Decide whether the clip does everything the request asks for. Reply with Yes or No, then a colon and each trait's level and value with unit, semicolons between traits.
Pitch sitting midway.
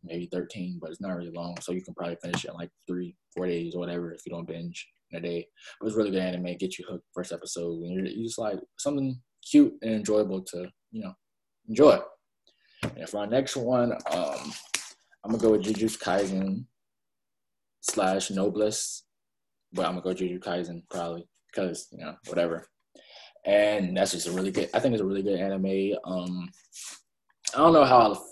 No: very low, 95 Hz